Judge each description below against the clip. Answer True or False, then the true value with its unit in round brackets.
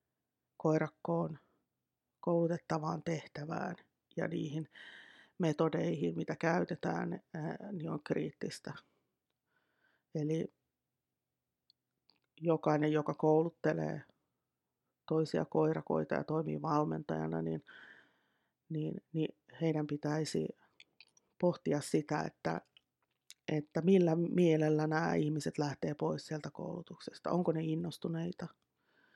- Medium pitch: True (155 Hz)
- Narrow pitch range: True (2.1 semitones)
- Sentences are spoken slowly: True (80 wpm)